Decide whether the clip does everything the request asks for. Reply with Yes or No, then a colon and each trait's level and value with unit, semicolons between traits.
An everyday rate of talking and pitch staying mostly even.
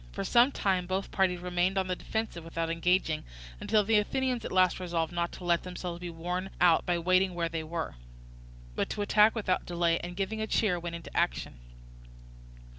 Yes: average, 190 wpm; narrow, 2.1 semitones